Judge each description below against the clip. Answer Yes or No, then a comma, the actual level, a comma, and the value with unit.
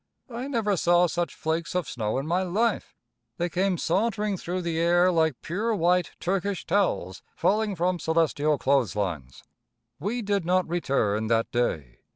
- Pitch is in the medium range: Yes, medium, 175 Hz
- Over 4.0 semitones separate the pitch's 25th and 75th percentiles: Yes, average, 5.3 semitones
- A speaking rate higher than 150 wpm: Yes, average, 160 wpm